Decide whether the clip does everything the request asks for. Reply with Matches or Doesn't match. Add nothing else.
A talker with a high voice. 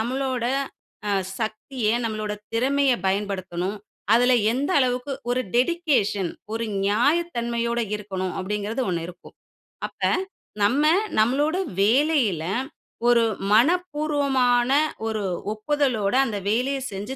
Matches